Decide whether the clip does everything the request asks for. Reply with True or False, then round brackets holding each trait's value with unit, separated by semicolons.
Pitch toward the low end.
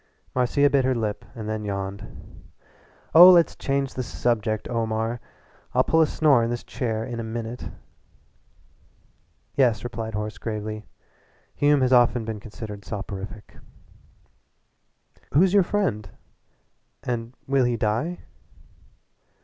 True (115 Hz)